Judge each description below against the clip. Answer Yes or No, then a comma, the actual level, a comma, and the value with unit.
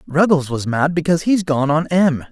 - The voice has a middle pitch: Yes, medium, 155 Hz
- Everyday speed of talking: No, fast, 210 wpm